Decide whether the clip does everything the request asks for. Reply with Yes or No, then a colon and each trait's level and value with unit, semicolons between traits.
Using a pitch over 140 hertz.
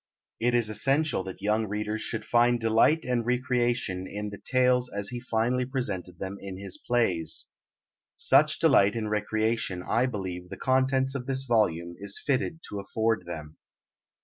No: low, 110 Hz